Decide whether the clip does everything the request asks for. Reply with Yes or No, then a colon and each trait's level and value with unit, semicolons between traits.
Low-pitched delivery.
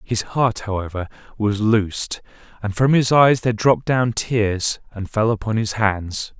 Yes: low, 110 Hz